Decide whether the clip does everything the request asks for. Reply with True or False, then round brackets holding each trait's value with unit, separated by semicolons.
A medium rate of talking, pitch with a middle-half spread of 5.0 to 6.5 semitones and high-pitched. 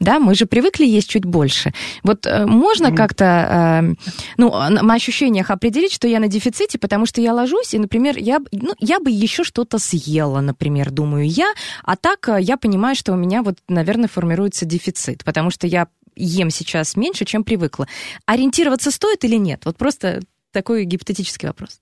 False (170 wpm; 5.3 semitones; 210 Hz)